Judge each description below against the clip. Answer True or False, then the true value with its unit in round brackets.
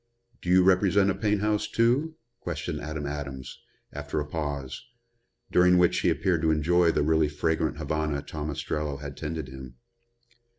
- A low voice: True (80 Hz)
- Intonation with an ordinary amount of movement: True (3.6 semitones)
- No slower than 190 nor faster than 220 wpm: False (160 wpm)